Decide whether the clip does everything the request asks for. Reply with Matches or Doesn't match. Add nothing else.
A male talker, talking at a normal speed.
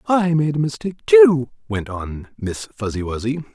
Matches